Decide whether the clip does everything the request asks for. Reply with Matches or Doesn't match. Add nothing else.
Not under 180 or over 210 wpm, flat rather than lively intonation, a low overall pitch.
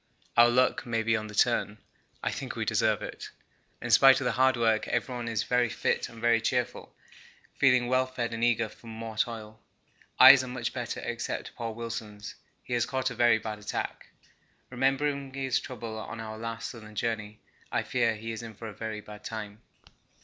Matches